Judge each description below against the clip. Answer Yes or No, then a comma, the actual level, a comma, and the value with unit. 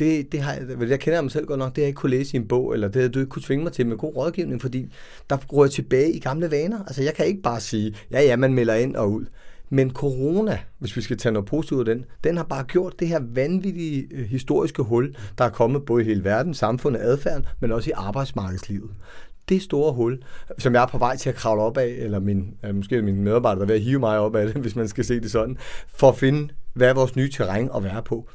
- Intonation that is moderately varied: Yes, average, 4.0 semitones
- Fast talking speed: Yes, fast, 275 wpm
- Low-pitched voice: Yes, low, 130 Hz